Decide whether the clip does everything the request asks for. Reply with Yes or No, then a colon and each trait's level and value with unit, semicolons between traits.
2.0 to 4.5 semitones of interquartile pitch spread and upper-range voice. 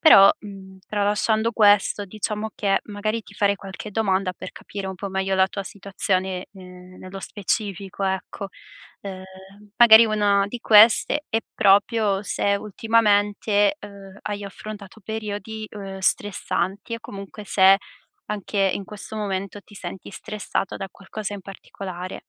No: narrow, 1.6 semitones; high, 200 Hz